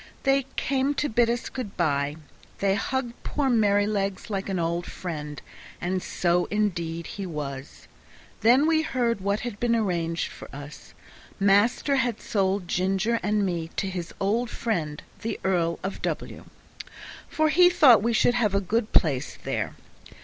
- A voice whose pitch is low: No, high, 200 Hz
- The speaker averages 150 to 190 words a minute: Yes, average, 155 wpm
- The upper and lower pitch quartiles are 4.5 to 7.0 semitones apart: Yes, wide, 5.4 semitones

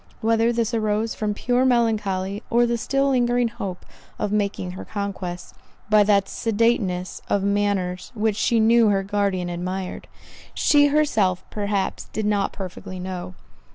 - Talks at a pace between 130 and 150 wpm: Yes, average, 145 wpm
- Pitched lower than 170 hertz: No, high, 205 Hz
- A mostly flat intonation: No, average, 3.3 semitones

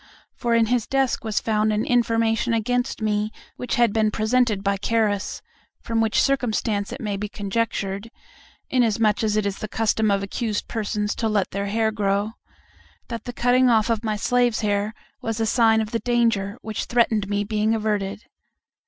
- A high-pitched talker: Yes, high, 220 Hz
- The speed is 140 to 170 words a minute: No, average, 180 wpm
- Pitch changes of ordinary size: No, narrow, 1.9 semitones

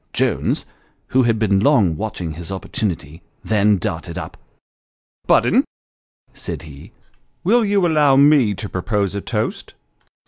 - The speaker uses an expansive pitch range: Yes, wide, 6.9 semitones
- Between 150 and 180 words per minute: No, average, 140 wpm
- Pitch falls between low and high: No, low, 105 Hz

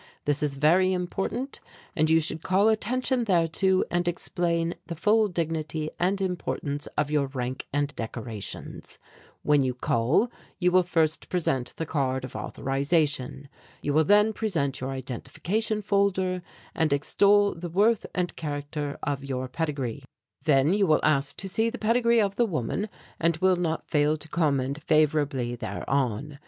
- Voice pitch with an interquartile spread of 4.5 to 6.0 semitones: Yes, average, 4.9 semitones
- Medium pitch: Yes, medium, 160 Hz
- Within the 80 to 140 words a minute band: No, average, 155 wpm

